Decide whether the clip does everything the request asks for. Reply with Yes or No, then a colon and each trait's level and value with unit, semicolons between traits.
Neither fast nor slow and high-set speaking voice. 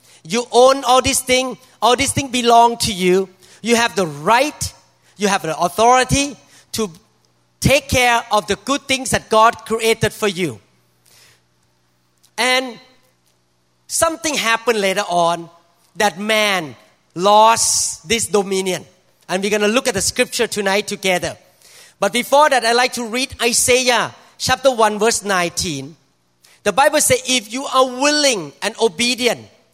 Yes: average, 145 wpm; high, 210 Hz